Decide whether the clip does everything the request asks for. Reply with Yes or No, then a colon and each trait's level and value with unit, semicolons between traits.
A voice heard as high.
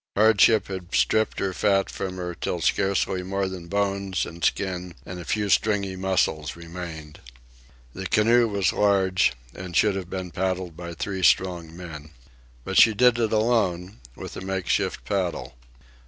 No: very low, 95 Hz